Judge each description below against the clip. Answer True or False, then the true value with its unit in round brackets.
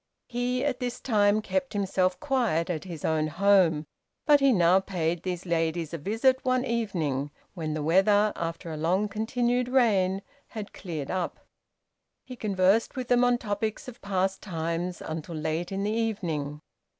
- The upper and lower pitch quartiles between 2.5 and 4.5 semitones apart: False (5.6 semitones)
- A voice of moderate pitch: False (195 Hz)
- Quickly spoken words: False (160 wpm)